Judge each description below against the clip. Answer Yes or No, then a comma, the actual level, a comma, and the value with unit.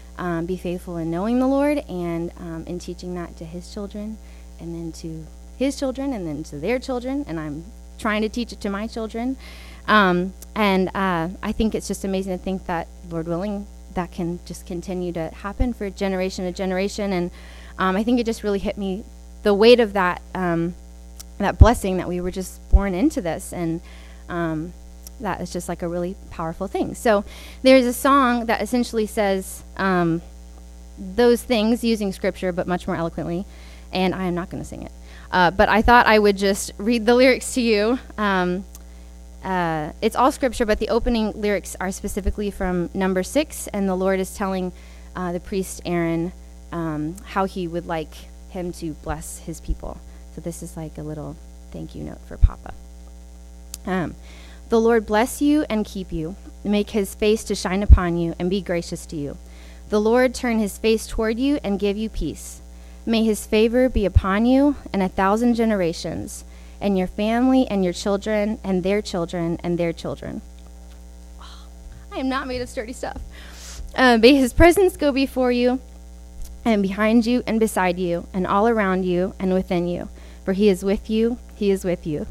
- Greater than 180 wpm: Yes, average, 190 wpm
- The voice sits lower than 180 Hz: No, medium, 185 Hz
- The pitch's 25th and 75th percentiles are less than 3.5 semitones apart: No, average, 4.8 semitones